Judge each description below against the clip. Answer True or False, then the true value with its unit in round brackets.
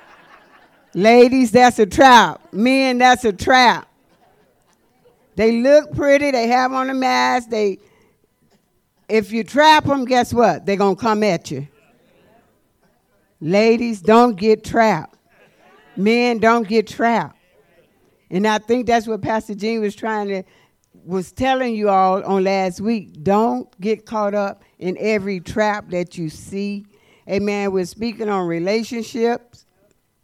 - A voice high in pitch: True (220 Hz)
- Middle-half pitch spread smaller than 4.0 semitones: True (3.3 semitones)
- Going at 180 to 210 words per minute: False (135 wpm)